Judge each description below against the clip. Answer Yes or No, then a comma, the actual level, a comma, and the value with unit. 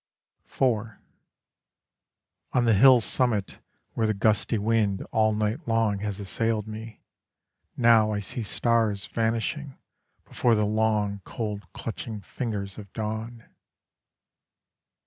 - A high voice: No, low, 110 Hz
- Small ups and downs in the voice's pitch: Yes, narrow, 1.7 semitones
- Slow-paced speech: Yes, slow, 110 wpm